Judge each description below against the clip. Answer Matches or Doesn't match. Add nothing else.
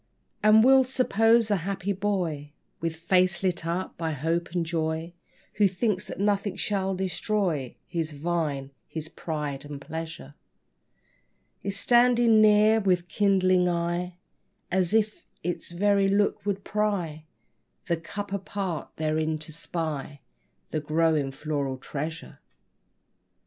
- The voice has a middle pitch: Matches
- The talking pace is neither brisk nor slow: Doesn't match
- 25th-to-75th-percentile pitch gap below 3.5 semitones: Doesn't match